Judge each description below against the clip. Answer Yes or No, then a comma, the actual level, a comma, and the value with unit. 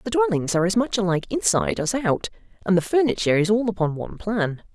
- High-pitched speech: Yes, high, 205 Hz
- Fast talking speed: Yes, fast, 215 wpm